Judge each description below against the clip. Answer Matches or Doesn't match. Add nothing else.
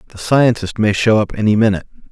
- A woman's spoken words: Doesn't match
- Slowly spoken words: Doesn't match